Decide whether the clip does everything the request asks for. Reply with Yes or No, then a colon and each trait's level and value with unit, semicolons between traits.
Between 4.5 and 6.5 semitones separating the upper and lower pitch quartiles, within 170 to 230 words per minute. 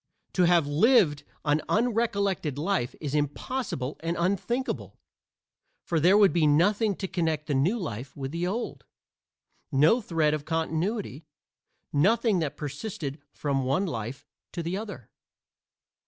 No: wide, 5.5 semitones; average, 140 wpm